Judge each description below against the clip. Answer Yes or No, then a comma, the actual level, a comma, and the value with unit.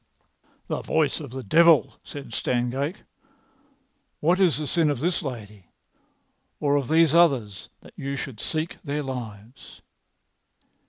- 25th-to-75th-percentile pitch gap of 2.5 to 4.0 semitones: No, average, 4.5 semitones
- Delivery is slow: Yes, slow, 130 wpm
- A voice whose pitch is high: No, medium, 140 Hz